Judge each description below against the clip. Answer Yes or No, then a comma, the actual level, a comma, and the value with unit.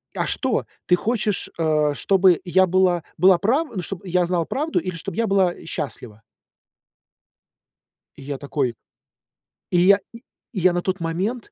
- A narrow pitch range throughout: No, average, 3.0 semitones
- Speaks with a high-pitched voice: No, medium, 180 Hz